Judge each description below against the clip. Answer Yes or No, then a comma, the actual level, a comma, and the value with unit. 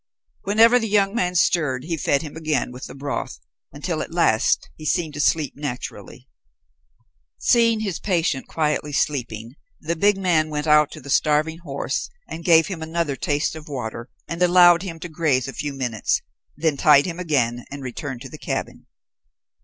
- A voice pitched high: No, medium, 155 Hz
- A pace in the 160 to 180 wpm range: Yes, average, 175 wpm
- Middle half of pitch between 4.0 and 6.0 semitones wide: No, average, 3.6 semitones